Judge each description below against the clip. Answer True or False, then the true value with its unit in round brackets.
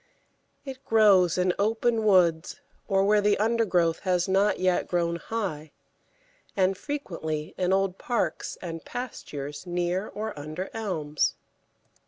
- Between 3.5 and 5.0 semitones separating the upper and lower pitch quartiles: True (3.9 semitones)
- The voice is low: False (185 Hz)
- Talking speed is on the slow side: True (125 wpm)